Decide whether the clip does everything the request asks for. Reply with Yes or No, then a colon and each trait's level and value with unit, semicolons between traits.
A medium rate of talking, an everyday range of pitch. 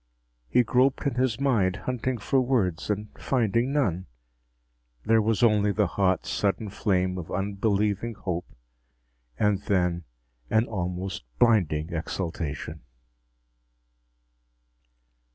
No: slow, 105 wpm; average, 4.2 semitones